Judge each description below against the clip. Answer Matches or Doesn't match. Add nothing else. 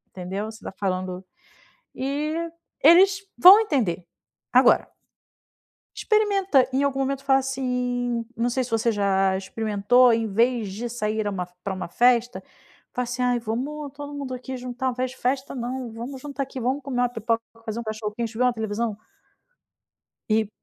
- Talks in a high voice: Matches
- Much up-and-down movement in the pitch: Doesn't match